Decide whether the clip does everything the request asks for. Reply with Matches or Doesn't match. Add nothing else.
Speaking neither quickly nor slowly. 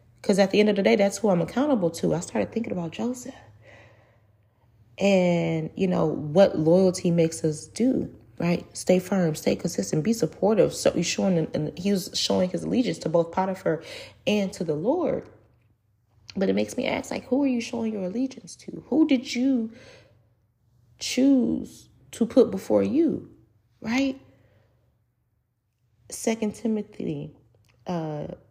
Matches